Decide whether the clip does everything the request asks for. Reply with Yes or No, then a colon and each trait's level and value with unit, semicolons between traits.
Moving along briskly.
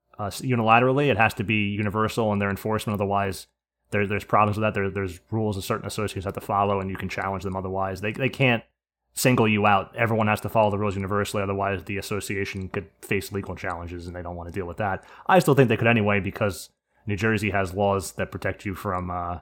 Yes: fast, 230 wpm